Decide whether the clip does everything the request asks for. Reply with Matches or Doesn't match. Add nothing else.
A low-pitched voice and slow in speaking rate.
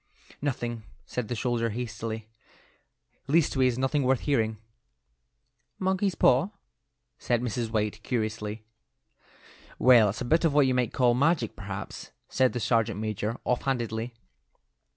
Matches